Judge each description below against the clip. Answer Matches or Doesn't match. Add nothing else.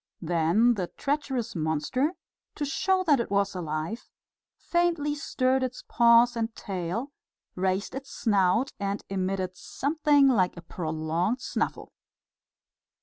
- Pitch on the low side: Doesn't match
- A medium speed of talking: Doesn't match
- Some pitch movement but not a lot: Doesn't match